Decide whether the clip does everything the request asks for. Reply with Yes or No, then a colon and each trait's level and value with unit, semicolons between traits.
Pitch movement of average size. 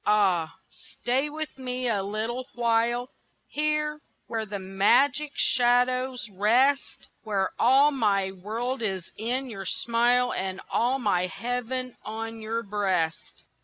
Yes: average, 3.8 semitones